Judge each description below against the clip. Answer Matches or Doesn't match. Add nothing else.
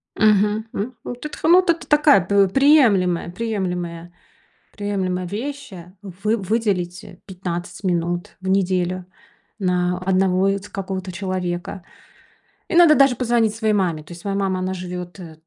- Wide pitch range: Doesn't match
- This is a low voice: Doesn't match